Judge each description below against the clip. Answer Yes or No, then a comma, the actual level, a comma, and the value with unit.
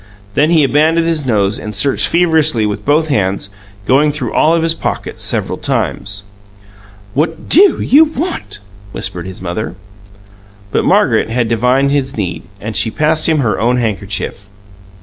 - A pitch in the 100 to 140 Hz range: Yes, low, 135 Hz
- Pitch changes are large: Yes, wide, 7.1 semitones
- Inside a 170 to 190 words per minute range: No, average, 155 wpm